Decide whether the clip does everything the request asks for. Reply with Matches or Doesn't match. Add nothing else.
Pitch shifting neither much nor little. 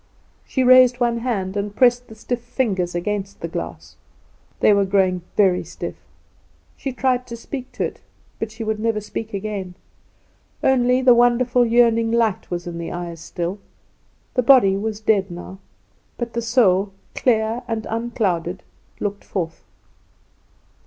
Matches